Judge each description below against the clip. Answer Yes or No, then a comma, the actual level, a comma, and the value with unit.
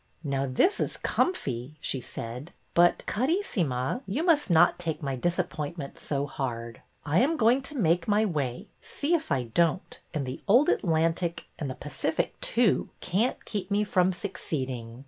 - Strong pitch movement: Yes, wide, 7.5 semitones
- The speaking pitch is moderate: Yes, medium, 165 Hz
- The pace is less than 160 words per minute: No, average, 165 wpm